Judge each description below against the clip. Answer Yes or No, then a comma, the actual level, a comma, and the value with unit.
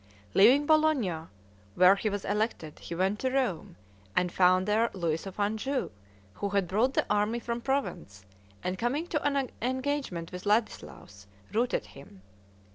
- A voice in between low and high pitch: No, high, 210 Hz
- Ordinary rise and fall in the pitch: No, wide, 6.2 semitones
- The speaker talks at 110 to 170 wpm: Yes, average, 150 wpm